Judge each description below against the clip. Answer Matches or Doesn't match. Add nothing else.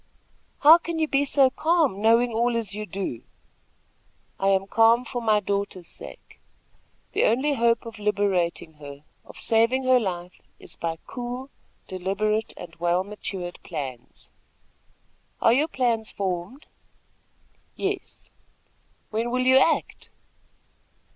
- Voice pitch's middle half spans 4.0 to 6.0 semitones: Matches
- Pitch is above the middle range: Matches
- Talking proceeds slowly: Matches